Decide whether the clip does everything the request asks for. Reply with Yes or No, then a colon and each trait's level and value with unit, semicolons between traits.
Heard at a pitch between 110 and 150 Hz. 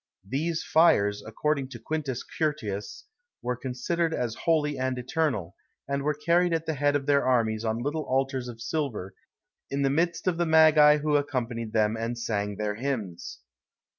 Yes: low, 135 Hz